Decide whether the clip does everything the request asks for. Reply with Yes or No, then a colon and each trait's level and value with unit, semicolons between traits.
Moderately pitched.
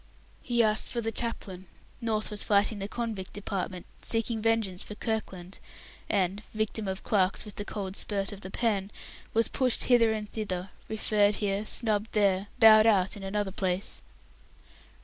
No: high, 210 Hz